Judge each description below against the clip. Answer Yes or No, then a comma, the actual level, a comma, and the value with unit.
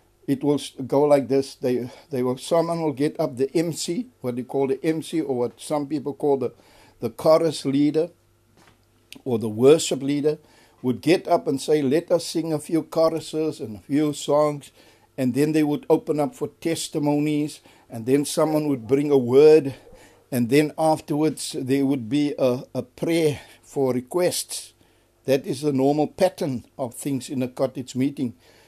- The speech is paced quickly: No, average, 180 wpm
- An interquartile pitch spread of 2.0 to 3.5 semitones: Yes, average, 3.2 semitones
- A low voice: No, medium, 145 Hz